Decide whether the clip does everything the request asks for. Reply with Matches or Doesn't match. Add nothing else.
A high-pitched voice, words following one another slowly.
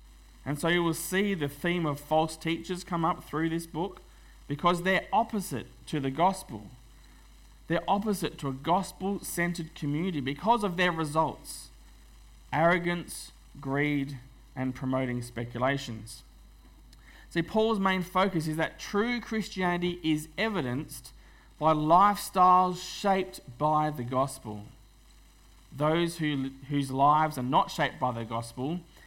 Doesn't match